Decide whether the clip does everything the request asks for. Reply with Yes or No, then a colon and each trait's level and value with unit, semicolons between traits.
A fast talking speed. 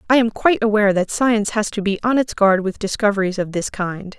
Yes: fast, 245 wpm